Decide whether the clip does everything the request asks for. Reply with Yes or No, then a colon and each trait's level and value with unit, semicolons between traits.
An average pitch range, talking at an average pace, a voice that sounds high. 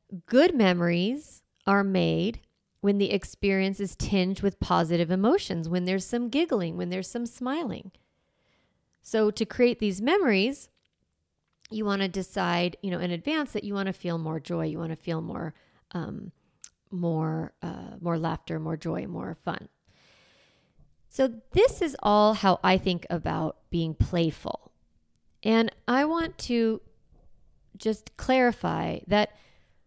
Yes: average, 4.6 semitones; average, 145 wpm; high, 195 Hz